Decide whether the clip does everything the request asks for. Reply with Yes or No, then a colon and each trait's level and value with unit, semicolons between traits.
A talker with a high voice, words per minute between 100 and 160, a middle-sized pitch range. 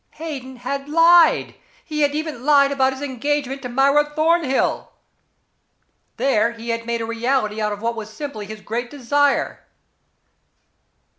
Yes: very high, 270 Hz; average, 145 wpm; average, 3.9 semitones